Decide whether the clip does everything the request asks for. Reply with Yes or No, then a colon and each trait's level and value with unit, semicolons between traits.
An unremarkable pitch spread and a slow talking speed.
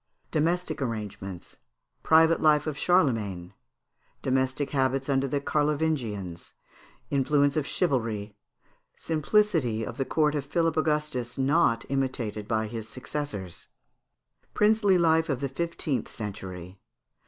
No: wide, 5.8 semitones; slow, 110 wpm